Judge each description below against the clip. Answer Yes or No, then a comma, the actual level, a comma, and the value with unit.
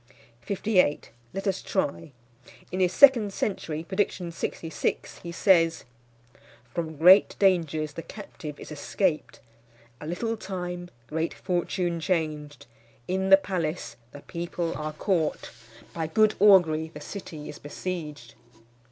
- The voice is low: No, medium, 170 Hz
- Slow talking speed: Yes, slow, 120 wpm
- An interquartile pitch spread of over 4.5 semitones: No, average, 3.5 semitones